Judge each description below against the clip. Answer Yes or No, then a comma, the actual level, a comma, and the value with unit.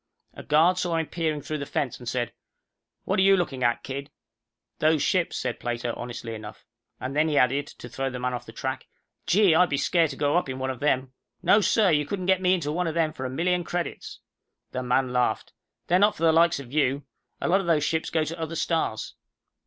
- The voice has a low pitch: No, medium, 150 Hz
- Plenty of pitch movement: No, average, 4.8 semitones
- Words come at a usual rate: No, fast, 235 wpm